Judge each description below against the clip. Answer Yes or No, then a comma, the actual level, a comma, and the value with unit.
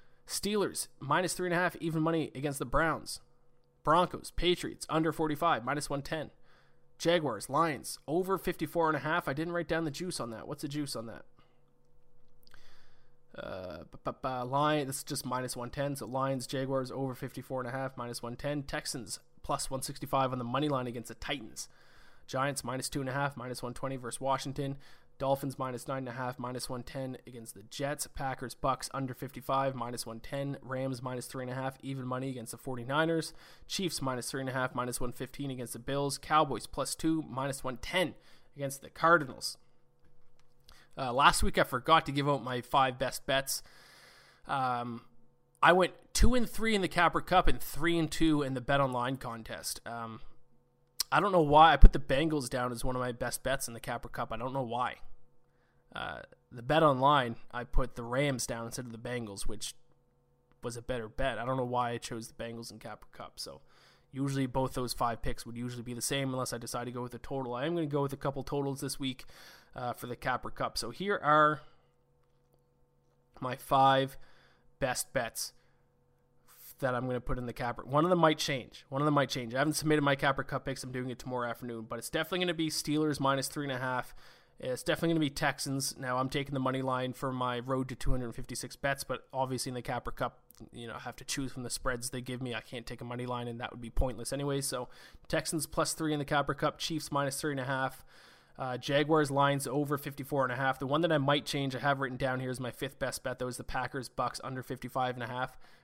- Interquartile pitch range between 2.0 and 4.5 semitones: Yes, average, 2.7 semitones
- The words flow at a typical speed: No, fast, 215 wpm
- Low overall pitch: Yes, low, 130 Hz